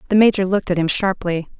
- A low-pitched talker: No, high, 190 Hz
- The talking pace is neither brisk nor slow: No, fast, 225 wpm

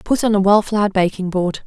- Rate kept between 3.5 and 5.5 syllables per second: No, 5.7 syllables/s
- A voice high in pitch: Yes, high, 200 Hz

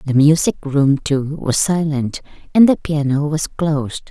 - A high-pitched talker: No, medium, 145 Hz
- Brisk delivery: No, average, 160 wpm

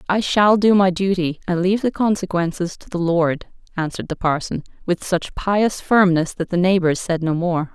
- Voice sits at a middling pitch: Yes, medium, 180 Hz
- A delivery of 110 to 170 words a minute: No, average, 195 wpm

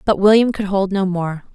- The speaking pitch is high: Yes, high, 195 Hz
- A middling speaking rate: No, fast, 235 wpm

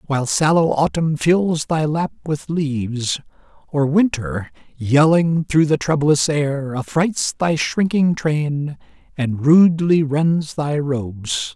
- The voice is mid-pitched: Yes, medium, 150 Hz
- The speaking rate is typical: No, slow, 125 wpm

